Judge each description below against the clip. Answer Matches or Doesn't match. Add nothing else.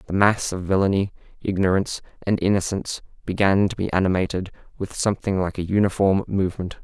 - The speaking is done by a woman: Doesn't match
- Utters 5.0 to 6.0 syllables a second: Doesn't match